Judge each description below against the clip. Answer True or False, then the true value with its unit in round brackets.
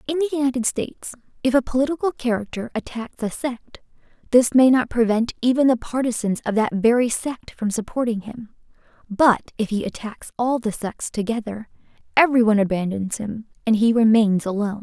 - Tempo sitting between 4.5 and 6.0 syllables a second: True (5.5 syllables/s)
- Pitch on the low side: False (235 Hz)